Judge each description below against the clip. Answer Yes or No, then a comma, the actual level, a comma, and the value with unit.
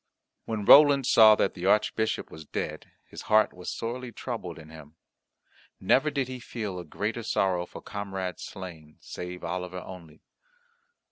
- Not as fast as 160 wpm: Yes, average, 150 wpm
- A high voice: No, very low, 95 Hz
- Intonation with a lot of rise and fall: No, average, 4.3 semitones